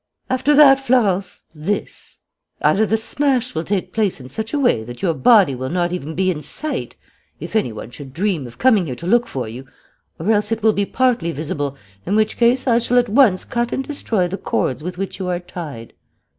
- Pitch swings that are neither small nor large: No, wide, 6.9 semitones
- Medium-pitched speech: No, high, 195 Hz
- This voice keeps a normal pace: No, fast, 215 wpm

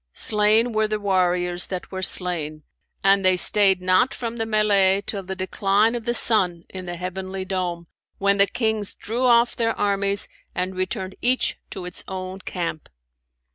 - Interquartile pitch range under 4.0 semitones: Yes, narrow, 2.6 semitones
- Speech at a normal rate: Yes, average, 170 wpm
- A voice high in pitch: Yes, high, 195 Hz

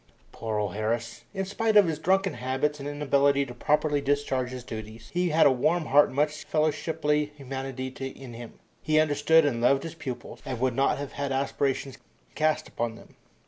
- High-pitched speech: No, medium, 140 Hz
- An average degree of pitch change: Yes, average, 3.1 semitones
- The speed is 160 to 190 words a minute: Yes, average, 185 wpm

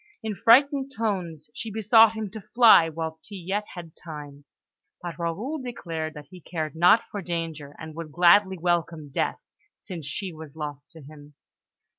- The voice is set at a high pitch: No, medium, 170 Hz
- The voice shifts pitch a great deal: No, average, 4.8 semitones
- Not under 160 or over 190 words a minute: Yes, average, 165 wpm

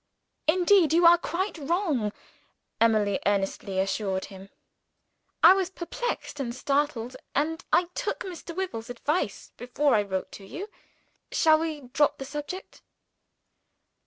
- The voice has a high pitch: Yes, very high, 290 Hz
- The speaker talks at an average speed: No, slow, 130 wpm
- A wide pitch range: Yes, wide, 7.5 semitones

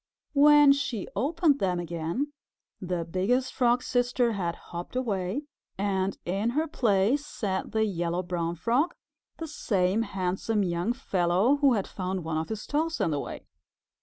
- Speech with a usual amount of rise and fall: No, wide, 6.4 semitones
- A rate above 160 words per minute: No, average, 155 wpm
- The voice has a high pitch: Yes, high, 205 Hz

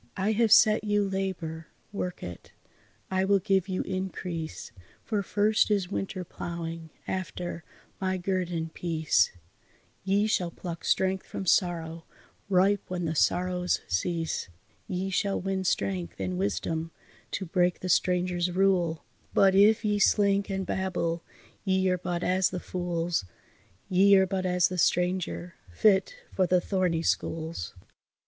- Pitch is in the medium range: Yes, medium, 180 Hz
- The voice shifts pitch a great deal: No, narrow, 2.4 semitones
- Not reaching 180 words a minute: Yes, average, 140 wpm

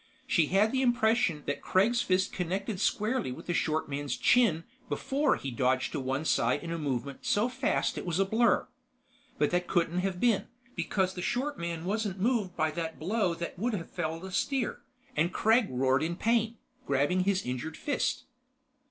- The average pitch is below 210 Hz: Yes, medium, 185 Hz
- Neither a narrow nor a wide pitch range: No, wide, 5.7 semitones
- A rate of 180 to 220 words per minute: Yes, average, 185 wpm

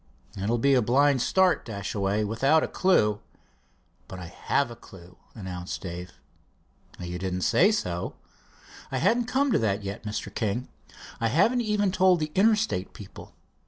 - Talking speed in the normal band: Yes, average, 160 wpm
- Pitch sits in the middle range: No, low, 115 Hz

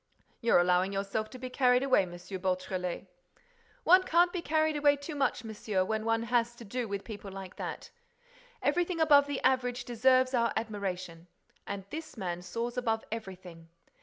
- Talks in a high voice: Yes, high, 230 Hz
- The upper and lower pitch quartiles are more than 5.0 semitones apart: Yes, wide, 5.4 semitones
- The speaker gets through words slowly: No, average, 165 wpm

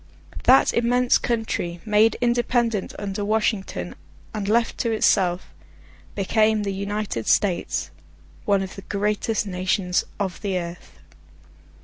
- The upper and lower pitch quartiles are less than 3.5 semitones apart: Yes, average, 2.7 semitones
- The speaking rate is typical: No, slow, 115 wpm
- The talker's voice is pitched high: Yes, high, 205 Hz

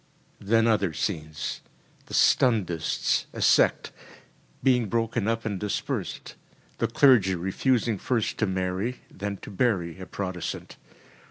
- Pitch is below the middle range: Yes, low, 100 Hz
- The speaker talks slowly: Yes, slow, 125 wpm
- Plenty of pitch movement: No, average, 3.7 semitones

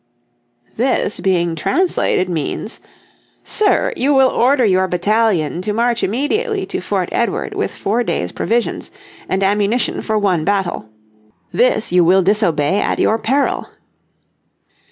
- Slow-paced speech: Yes, slow, 130 wpm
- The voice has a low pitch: No, high, 210 Hz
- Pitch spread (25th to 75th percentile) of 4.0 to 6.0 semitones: Yes, average, 5.1 semitones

